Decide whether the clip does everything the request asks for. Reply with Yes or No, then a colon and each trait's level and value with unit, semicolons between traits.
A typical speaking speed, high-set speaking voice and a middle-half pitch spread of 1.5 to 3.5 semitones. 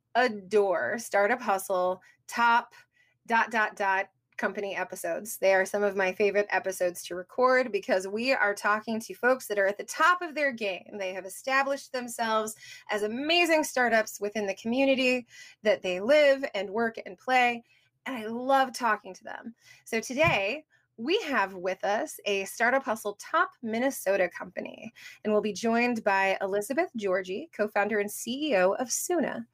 No: average, 165 wpm; high, 215 Hz; average, 4.5 semitones